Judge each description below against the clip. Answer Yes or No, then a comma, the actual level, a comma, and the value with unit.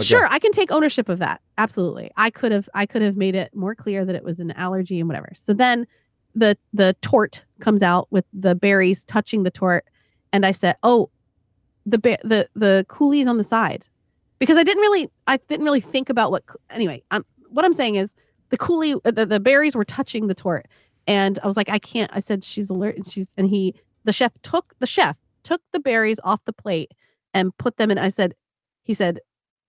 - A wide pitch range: No, average, 4.4 semitones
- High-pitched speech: Yes, high, 210 Hz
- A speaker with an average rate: No, fast, 220 wpm